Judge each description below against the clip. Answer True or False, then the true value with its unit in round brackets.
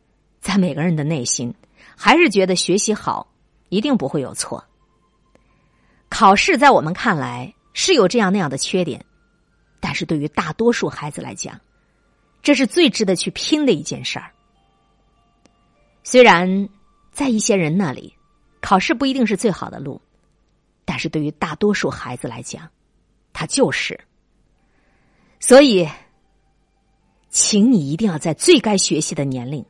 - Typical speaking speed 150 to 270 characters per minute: True (215 characters per minute)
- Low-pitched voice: False (195 Hz)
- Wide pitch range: True (6.5 semitones)